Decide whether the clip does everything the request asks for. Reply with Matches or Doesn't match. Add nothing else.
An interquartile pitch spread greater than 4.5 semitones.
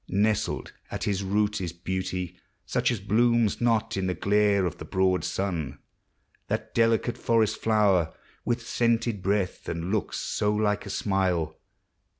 Doesn't match